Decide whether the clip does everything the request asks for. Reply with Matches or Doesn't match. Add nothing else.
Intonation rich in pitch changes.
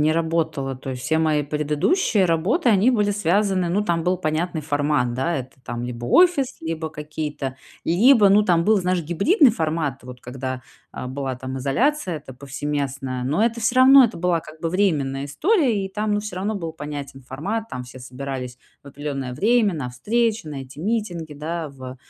Matches